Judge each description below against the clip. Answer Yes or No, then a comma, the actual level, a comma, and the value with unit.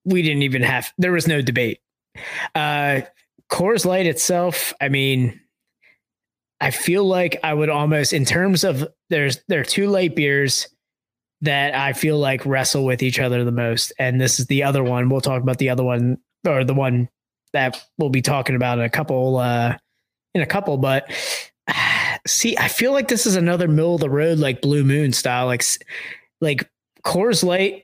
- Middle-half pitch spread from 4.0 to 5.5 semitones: Yes, average, 5.0 semitones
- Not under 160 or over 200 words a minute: Yes, average, 190 wpm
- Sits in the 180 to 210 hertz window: No, medium, 140 Hz